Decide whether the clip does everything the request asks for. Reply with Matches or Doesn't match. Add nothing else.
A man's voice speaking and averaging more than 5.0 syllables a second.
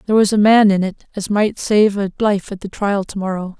Doesn't match